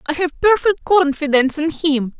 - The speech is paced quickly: No, average, 165 wpm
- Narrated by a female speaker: Yes, female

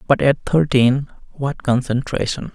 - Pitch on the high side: No, low, 135 Hz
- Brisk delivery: No, slow, 95 wpm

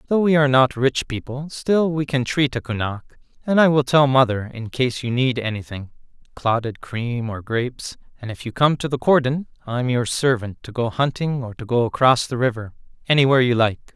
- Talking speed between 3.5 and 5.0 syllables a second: No, 5.4 syllables/s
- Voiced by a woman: No, male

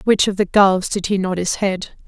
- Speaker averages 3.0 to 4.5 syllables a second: No, 5.1 syllables/s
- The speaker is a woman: Yes, female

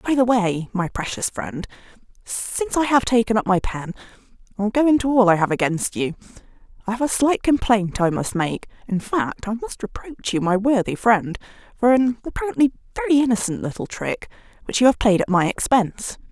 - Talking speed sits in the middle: Yes, average, 185 wpm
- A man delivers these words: No, female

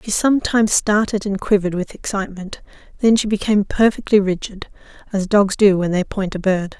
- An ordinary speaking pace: Yes, average, 175 wpm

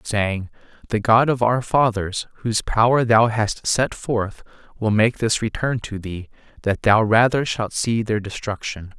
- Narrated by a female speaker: No, male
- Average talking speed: Yes, average, 165 wpm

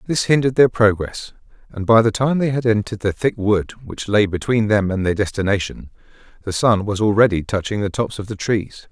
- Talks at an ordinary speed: No, fast, 210 wpm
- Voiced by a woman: No, male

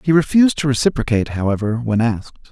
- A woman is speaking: No, male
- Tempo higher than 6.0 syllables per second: Yes, 7.0 syllables/s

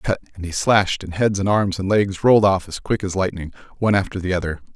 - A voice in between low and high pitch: No, very low, 95 Hz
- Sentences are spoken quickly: Yes, fast, 265 wpm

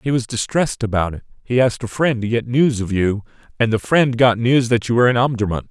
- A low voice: Yes, low, 120 Hz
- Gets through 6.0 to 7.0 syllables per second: Yes, 6.1 syllables/s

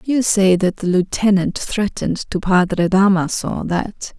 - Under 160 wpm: Yes, average, 145 wpm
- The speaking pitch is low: No, high, 190 Hz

